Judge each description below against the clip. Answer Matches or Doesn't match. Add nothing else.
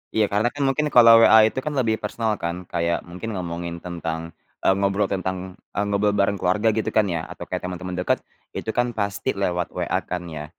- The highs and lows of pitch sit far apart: Doesn't match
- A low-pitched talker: Matches